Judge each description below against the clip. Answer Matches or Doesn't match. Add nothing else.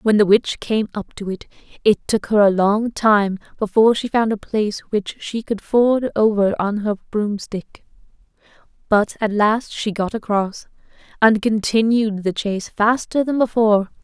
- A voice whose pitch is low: Doesn't match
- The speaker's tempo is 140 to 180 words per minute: Matches